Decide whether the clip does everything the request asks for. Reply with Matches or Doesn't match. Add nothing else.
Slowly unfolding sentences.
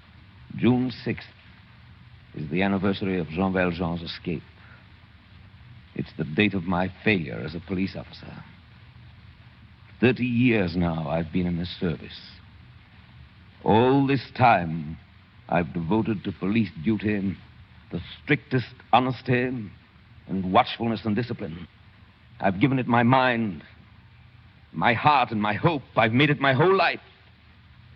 Matches